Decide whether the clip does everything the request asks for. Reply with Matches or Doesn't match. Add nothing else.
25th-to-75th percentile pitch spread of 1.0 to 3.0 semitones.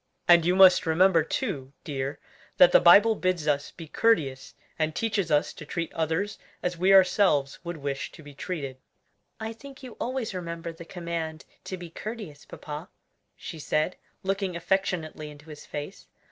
Doesn't match